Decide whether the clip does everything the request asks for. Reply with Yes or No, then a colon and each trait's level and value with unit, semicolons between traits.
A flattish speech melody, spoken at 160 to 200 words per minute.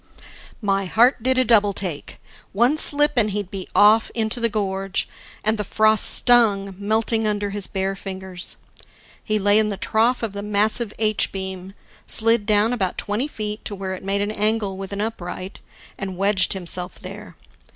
Yes: narrow, 2.2 semitones; average, 175 wpm